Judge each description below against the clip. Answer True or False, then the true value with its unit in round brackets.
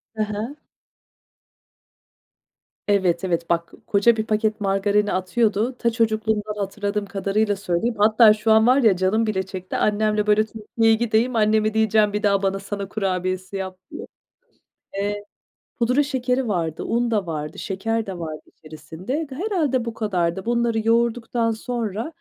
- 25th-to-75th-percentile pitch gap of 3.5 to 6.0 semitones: False (2.8 semitones)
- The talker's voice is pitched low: False (215 Hz)